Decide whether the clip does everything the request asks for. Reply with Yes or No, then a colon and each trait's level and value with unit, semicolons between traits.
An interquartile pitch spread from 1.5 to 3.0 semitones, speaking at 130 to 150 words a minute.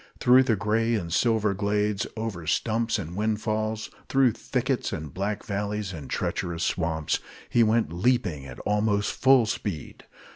No: average, 3.9 semitones; average, 145 wpm